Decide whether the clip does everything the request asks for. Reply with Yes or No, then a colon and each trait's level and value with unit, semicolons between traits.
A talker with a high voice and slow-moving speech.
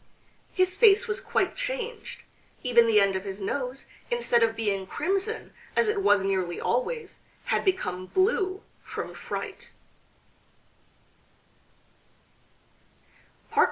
Yes: very high, 275 Hz; slow, 110 wpm